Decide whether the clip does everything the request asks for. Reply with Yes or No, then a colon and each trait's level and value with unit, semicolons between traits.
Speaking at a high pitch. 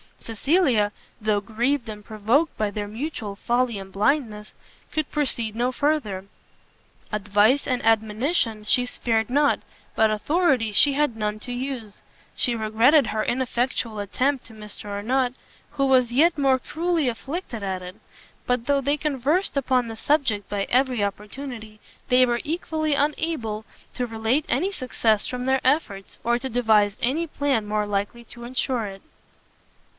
Yes: high, 240 Hz